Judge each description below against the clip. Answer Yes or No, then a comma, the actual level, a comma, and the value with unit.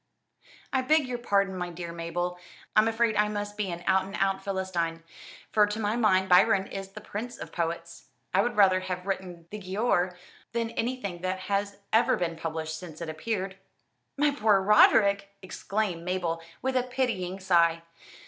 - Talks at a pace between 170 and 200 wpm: Yes, average, 175 wpm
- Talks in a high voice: Yes, high, 195 Hz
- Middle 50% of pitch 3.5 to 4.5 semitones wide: No, average, 3.1 semitones